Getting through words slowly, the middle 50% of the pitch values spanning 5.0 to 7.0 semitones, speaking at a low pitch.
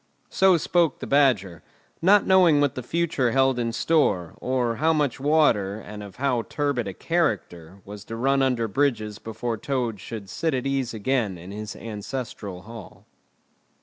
No: average, 165 wpm; wide, 5.4 semitones; low, 120 Hz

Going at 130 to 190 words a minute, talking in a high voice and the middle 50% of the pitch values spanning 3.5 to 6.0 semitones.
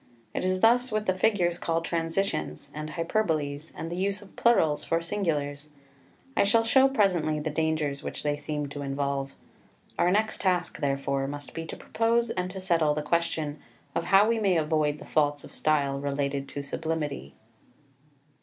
No: average, 170 wpm; medium, 160 Hz; average, 4.7 semitones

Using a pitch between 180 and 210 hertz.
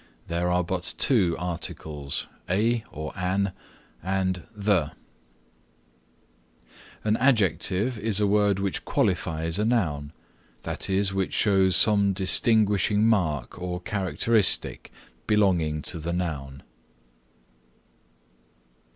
No: very low, 95 Hz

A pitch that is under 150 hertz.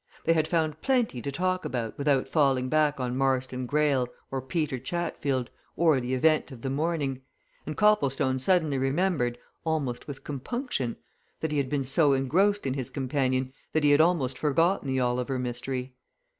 Yes: medium, 140 Hz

